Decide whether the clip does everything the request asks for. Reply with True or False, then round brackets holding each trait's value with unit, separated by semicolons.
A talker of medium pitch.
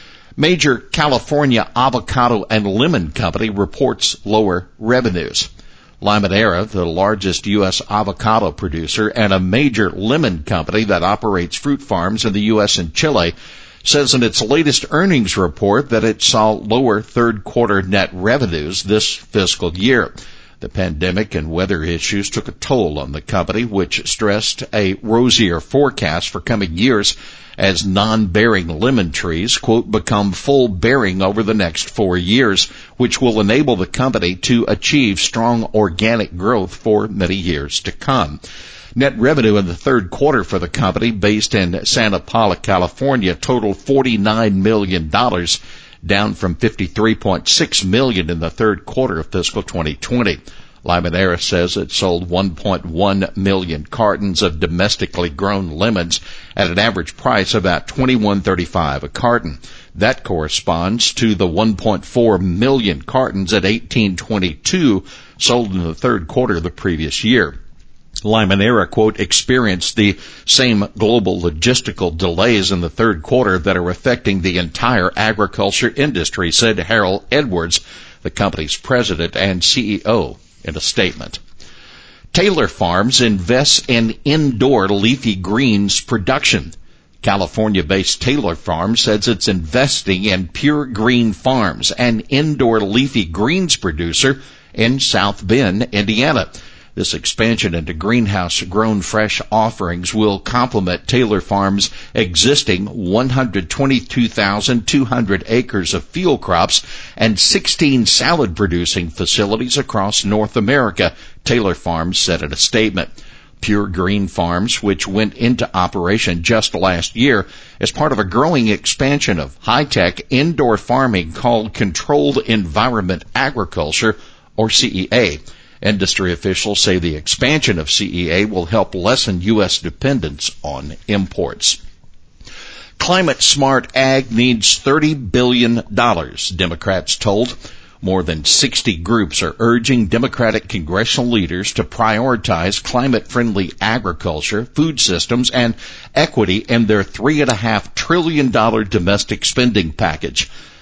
False (105 Hz)